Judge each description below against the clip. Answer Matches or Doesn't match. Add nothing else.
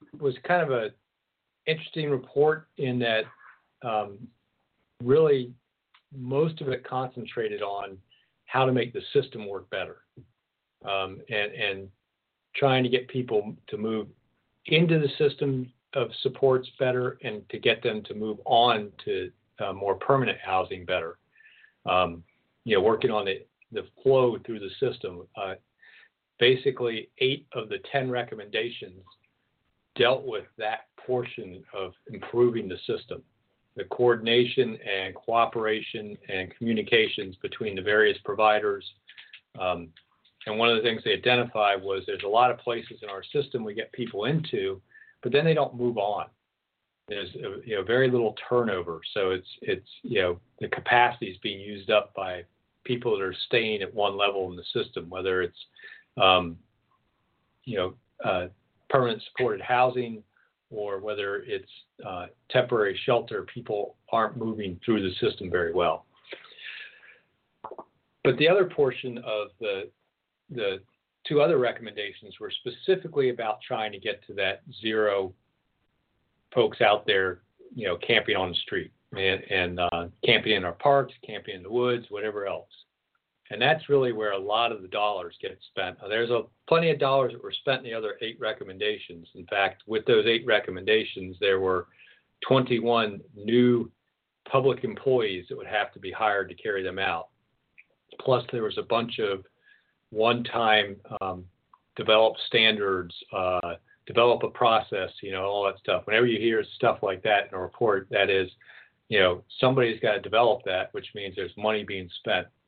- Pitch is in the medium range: Doesn't match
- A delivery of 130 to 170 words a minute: Matches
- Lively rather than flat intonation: Matches